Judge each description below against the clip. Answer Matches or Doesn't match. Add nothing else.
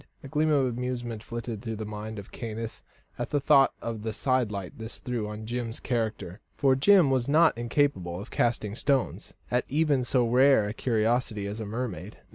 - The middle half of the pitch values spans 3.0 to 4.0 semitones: Matches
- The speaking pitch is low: Matches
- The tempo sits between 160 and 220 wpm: Matches